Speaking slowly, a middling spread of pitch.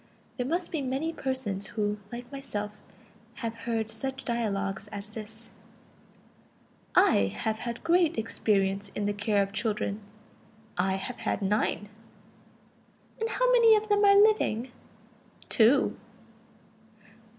Yes: slow, 125 wpm; average, 4.9 semitones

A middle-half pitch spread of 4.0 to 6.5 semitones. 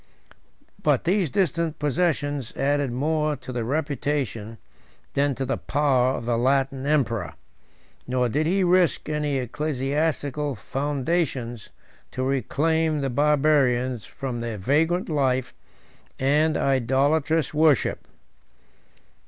No: average, 3.1 semitones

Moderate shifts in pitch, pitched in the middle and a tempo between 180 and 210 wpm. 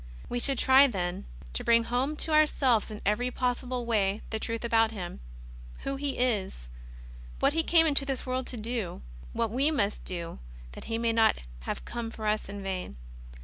No: average, 4.2 semitones; high, 230 Hz; average, 190 wpm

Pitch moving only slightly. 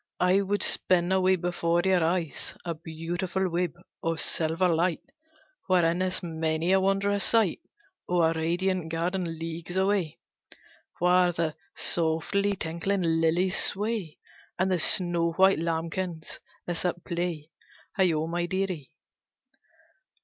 Yes: narrow, 2.3 semitones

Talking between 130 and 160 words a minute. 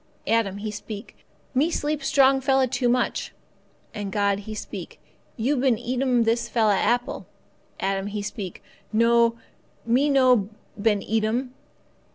Yes: average, 145 wpm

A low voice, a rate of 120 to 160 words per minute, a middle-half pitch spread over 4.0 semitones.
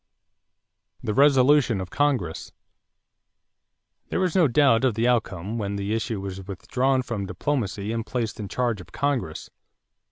Yes: low, 115 Hz; average, 140 wpm; average, 4.9 semitones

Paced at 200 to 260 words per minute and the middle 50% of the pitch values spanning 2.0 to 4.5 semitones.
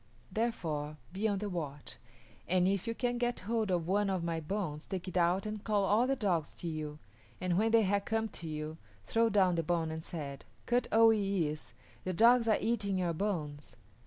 No: fast, 205 wpm; average, 4.9 semitones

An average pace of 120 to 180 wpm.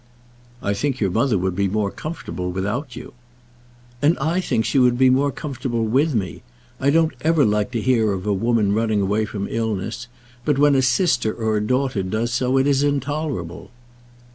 No: average, 190 wpm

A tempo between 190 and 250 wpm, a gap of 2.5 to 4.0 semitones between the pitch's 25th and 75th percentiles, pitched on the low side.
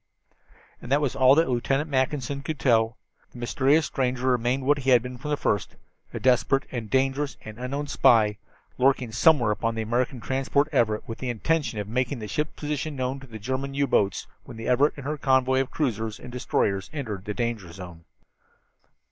Yes: average, 195 wpm; average, 3.3 semitones; low, 130 Hz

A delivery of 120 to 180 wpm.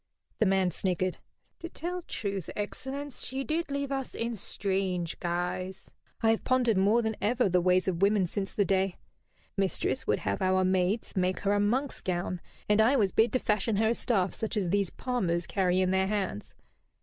No: average, 195 wpm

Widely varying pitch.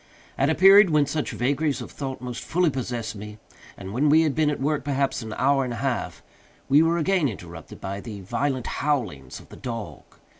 No: average, 4.7 semitones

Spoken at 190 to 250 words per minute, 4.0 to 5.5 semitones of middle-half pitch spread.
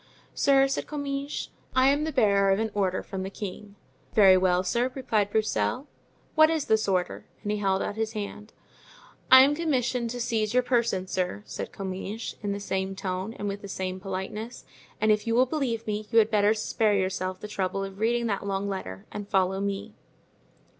No: average, 195 wpm; average, 3.5 semitones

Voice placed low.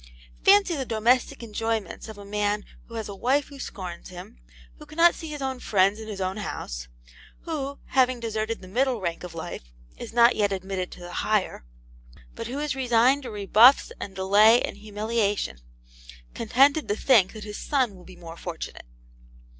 No: high, 220 Hz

